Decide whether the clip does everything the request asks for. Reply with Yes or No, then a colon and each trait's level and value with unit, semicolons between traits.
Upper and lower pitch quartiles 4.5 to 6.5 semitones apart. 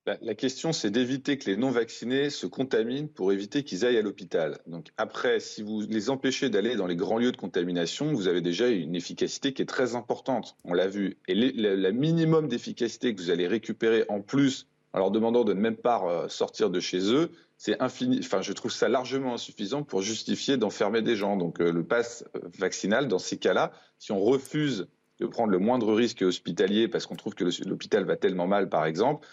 Yes: average, 5.2 semitones